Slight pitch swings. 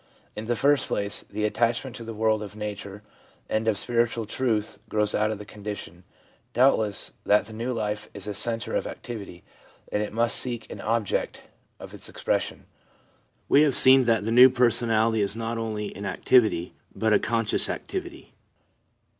Yes: narrow, 2.1 semitones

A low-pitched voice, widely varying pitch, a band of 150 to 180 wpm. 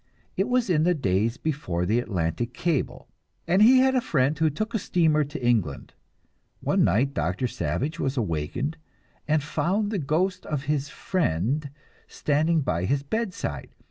No: medium, 145 Hz; wide, 6.6 semitones; average, 160 wpm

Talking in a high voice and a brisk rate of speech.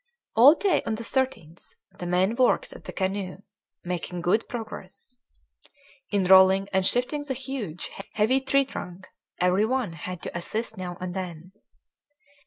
No: high, 195 Hz; average, 150 wpm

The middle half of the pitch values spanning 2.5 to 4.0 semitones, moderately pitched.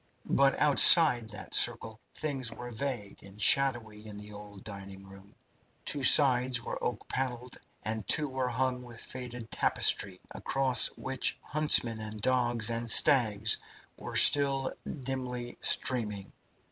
No: average, 3.6 semitones; low, 120 Hz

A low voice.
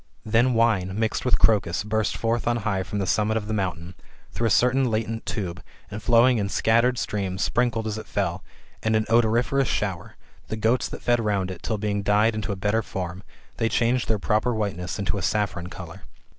Yes: low, 110 Hz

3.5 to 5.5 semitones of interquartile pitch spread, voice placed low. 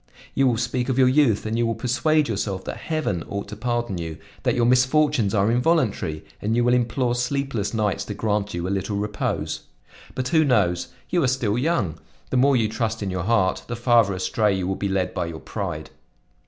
Yes: average, 4.1 semitones; low, 115 Hz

